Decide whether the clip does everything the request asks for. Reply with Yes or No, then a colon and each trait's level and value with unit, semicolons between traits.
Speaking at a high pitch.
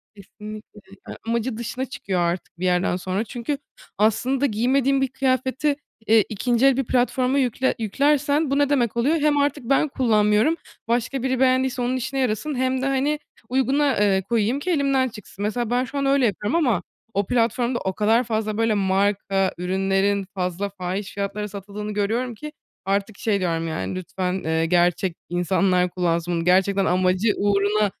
Yes: high, 220 Hz